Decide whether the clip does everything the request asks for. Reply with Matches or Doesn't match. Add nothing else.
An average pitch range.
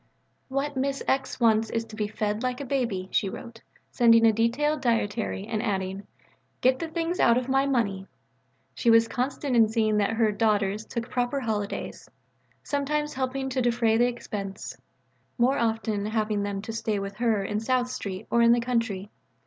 Matches